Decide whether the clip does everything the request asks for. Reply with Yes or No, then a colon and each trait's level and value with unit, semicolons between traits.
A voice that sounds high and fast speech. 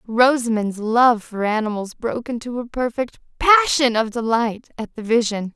No: high, 235 Hz; average, 150 wpm